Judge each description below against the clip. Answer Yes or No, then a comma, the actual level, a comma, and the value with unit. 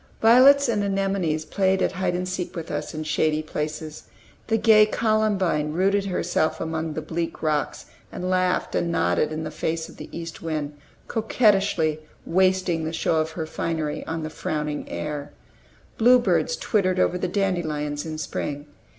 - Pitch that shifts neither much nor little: Yes, average, 3.8 semitones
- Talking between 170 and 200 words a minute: No, average, 160 wpm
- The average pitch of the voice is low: No, medium, 165 Hz